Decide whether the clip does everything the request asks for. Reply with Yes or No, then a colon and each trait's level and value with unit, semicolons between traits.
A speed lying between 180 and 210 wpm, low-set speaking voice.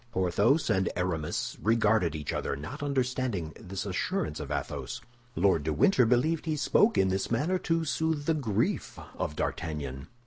No: average, 160 wpm; low, 105 Hz